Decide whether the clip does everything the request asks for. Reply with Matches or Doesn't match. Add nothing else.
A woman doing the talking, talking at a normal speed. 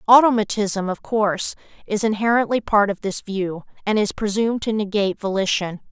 Matches